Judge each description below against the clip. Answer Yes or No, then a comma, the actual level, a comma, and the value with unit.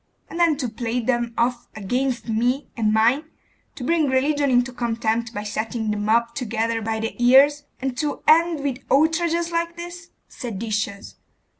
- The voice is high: Yes, high, 245 Hz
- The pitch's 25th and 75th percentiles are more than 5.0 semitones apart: No, average, 4.5 semitones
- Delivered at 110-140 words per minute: No, average, 160 wpm